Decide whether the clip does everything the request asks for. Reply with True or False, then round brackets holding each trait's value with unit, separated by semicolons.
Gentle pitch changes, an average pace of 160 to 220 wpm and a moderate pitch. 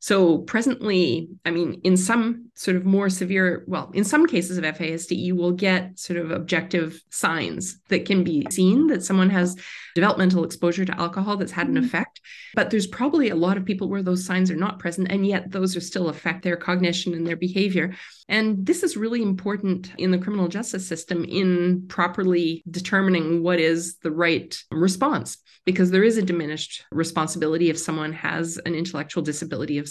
True (2.3 semitones; 185 wpm; 180 Hz)